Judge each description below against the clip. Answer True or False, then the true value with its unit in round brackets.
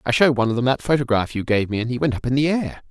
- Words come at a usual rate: False (350 wpm)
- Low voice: True (125 Hz)